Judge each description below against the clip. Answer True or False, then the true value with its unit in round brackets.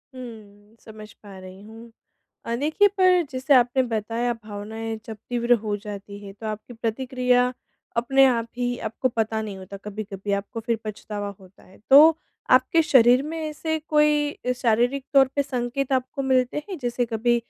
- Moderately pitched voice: False (240 Hz)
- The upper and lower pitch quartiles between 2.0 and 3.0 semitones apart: False (3.7 semitones)